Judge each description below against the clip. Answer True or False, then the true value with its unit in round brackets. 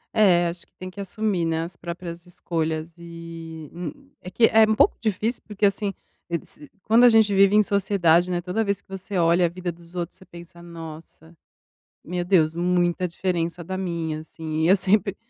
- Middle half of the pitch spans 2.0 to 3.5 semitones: True (2.9 semitones)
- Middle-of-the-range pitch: True (175 Hz)